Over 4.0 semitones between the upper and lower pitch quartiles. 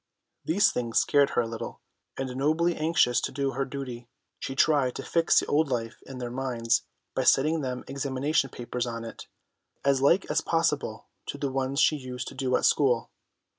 No: average, 2.8 semitones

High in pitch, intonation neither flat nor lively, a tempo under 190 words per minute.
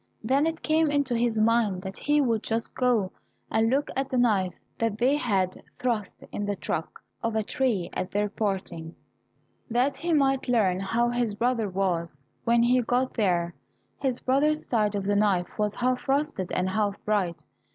Yes: high, 225 Hz; average, 4.4 semitones; average, 180 wpm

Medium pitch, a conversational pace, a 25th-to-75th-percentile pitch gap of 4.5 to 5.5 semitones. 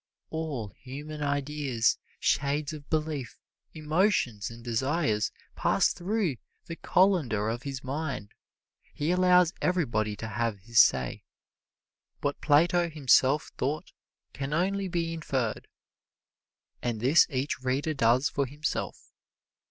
No: medium, 145 Hz; slow, 115 wpm; average, 4.8 semitones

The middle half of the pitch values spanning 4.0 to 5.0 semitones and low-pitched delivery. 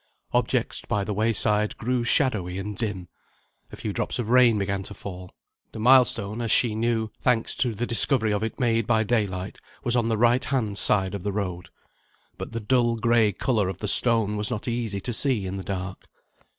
No: average, 3.0 semitones; low, 110 Hz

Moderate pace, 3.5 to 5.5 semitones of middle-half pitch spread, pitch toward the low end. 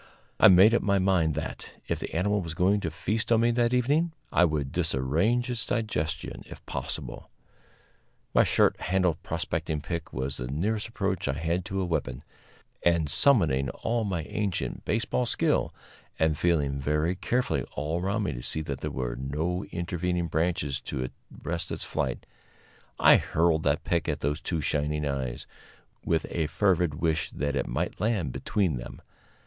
Yes: average, 170 wpm; average, 5.0 semitones; very low, 85 Hz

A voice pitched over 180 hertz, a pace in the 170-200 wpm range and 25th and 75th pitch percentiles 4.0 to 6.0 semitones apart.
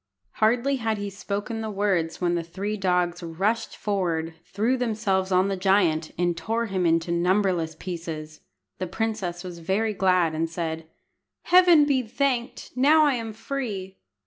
No: high, 190 Hz; average, 155 wpm; average, 4.5 semitones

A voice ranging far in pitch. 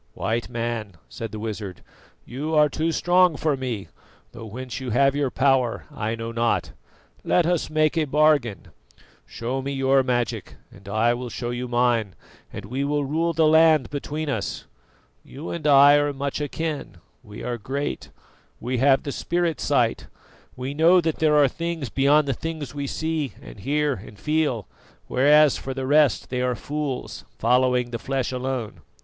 No: average, 3.9 semitones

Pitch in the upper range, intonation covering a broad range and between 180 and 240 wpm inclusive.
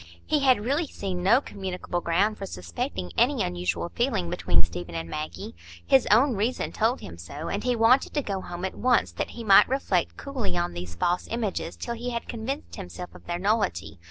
Yes: high, 195 Hz; wide, 8.7 semitones; average, 200 wpm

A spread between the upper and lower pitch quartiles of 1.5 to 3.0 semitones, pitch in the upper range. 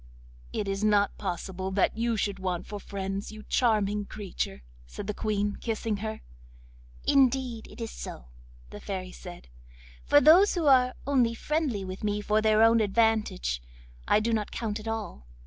Yes: average, 2.7 semitones; high, 215 Hz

